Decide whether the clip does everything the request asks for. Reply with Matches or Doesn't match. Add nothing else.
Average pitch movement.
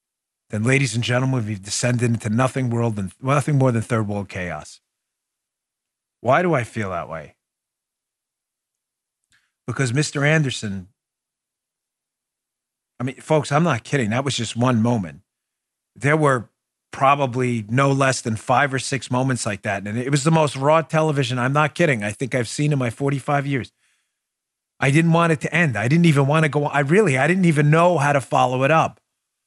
Matches